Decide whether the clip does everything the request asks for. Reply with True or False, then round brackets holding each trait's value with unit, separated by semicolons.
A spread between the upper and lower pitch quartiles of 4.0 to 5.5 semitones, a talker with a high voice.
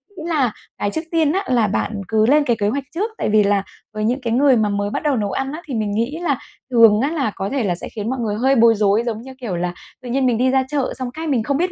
True (4.7 semitones; 240 Hz)